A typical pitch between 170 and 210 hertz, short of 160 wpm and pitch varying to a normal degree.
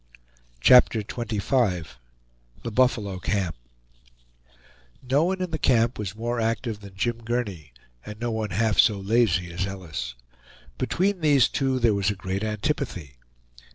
No: low, 110 Hz; average, 140 wpm; average, 4.1 semitones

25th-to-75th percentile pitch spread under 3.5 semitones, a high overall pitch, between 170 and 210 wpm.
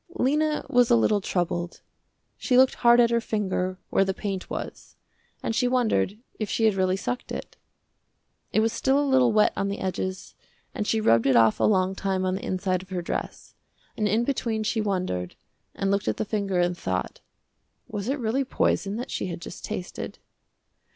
No: average, 4.0 semitones; high, 200 Hz; average, 195 wpm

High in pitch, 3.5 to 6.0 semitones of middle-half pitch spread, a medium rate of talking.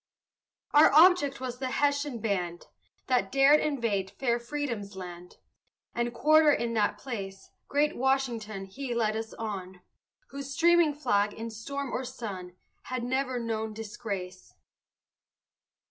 No: high, 235 Hz; average, 5.1 semitones; slow, 130 wpm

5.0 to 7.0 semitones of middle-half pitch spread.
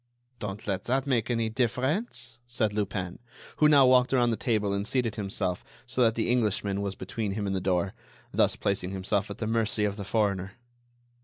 No: average, 3.5 semitones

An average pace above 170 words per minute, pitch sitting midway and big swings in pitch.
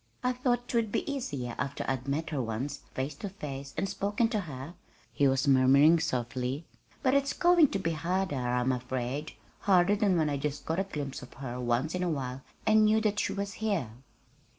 Yes: average, 200 wpm; medium, 155 Hz; wide, 7.3 semitones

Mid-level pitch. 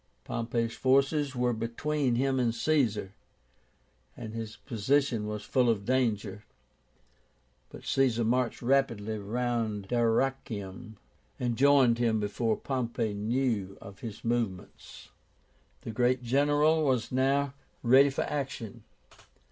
No: low, 120 Hz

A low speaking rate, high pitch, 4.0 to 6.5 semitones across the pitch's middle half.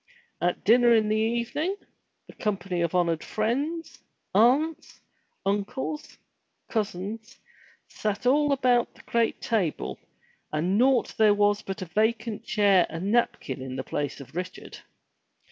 Yes: slow, 130 wpm; high, 215 Hz; average, 4.3 semitones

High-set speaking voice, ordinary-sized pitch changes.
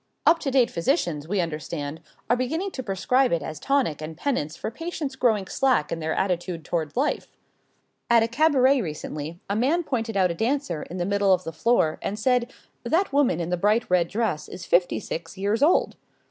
No: high, 205 Hz; wide, 7.5 semitones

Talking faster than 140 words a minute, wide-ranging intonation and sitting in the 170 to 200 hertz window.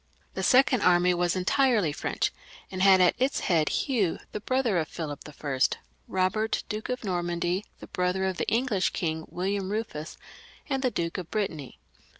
No: average, 170 wpm; average, 4.0 semitones; medium, 185 Hz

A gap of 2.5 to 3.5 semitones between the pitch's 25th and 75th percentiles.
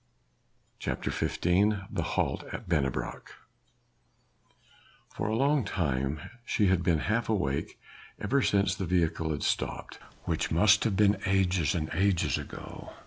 No: average, 4.2 semitones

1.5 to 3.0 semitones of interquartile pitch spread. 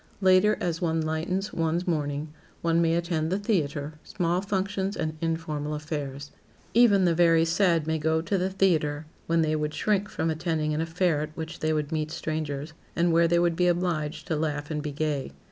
Yes: narrow, 2.4 semitones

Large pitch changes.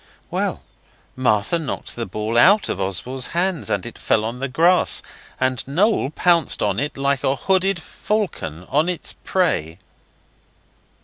Yes: wide, 7.5 semitones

